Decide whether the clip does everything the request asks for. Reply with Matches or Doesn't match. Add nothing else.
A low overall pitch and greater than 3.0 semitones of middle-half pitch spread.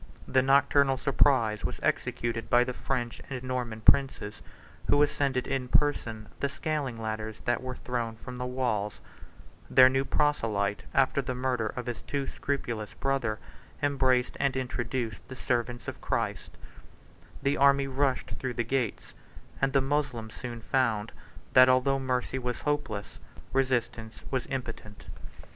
Doesn't match